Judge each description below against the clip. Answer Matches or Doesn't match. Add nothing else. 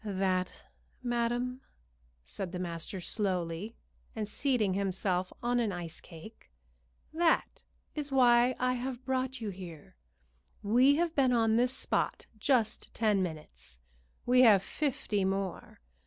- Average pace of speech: Doesn't match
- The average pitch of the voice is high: Matches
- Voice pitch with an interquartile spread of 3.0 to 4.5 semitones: Doesn't match